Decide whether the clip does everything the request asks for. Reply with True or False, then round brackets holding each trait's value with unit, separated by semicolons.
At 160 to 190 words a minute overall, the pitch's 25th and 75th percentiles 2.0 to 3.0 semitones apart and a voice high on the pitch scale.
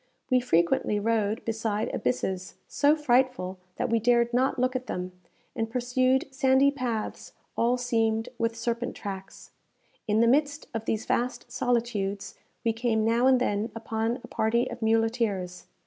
False (150 wpm; 2.4 semitones; 230 Hz)